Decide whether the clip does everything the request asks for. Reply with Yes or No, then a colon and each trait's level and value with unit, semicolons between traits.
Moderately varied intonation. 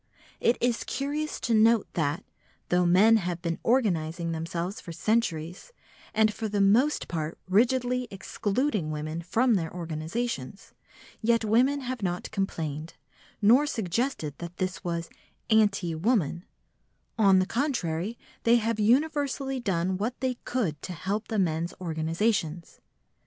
No: wide, 5.7 semitones